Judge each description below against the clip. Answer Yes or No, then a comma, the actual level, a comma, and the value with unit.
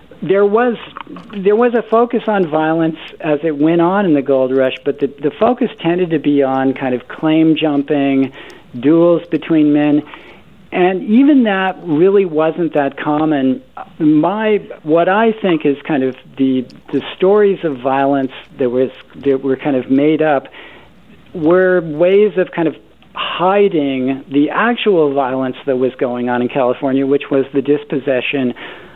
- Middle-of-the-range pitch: Yes, medium, 155 Hz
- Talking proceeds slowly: No, average, 160 wpm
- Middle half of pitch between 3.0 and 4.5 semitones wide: No, average, 5.1 semitones